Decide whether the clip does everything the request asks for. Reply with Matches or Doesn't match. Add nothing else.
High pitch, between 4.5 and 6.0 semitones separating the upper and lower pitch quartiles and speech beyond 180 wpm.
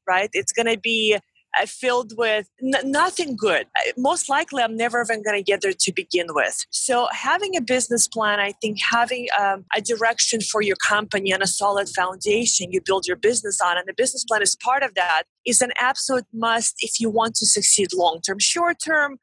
Doesn't match